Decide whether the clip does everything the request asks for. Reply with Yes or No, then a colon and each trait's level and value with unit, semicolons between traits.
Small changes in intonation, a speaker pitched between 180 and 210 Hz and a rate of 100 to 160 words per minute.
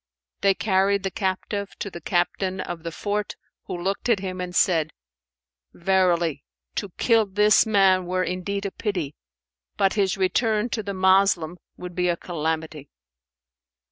Yes: narrow, 2.3 semitones; high, 190 Hz; average, 150 wpm